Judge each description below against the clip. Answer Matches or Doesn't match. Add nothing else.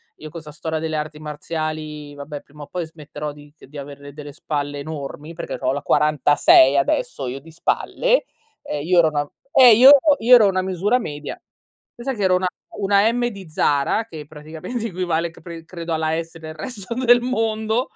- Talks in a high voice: Doesn't match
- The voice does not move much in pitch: Doesn't match